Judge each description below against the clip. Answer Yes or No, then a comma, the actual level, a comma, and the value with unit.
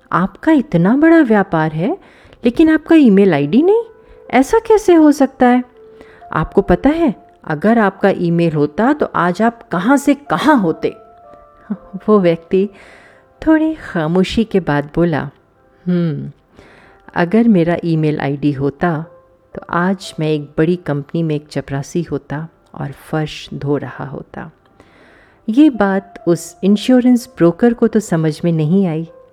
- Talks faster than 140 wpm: No, average, 135 wpm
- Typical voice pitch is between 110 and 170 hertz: No, medium, 185 Hz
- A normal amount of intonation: No, wide, 7.4 semitones